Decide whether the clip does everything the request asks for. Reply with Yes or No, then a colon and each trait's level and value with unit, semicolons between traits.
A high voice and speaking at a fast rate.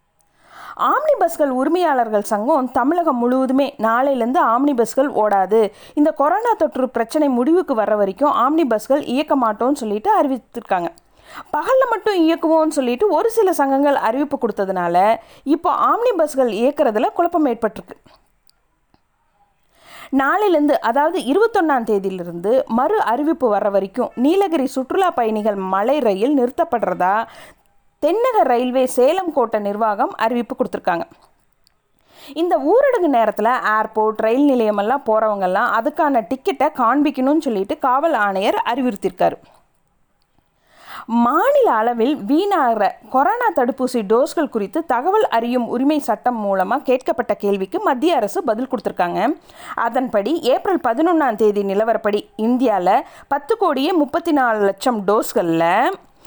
No: very high, 265 Hz; average, 110 wpm